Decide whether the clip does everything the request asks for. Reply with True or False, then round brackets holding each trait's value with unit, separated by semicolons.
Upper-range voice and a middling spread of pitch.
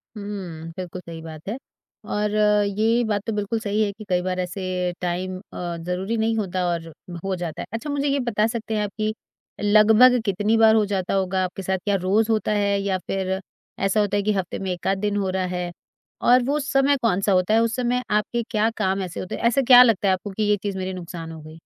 True (200 Hz; 3.0 semitones)